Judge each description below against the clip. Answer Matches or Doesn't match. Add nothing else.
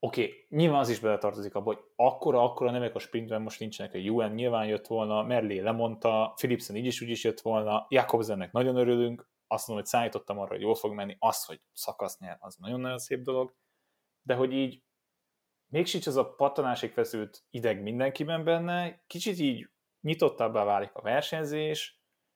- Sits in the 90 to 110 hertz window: Doesn't match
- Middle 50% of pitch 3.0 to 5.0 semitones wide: Matches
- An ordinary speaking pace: Doesn't match